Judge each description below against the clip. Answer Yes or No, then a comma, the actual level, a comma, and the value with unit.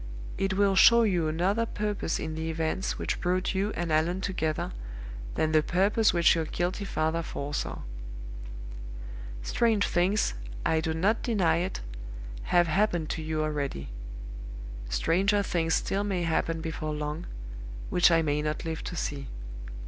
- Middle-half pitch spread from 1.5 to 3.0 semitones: No, average, 3.5 semitones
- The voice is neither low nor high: Yes, medium, 170 Hz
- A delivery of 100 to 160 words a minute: Yes, average, 150 wpm